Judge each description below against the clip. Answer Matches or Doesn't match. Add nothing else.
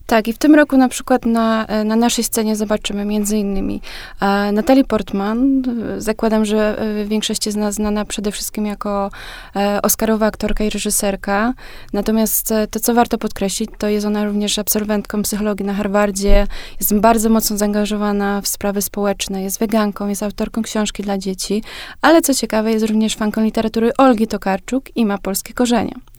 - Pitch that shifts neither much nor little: Doesn't match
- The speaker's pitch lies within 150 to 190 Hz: Doesn't match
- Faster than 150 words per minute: Matches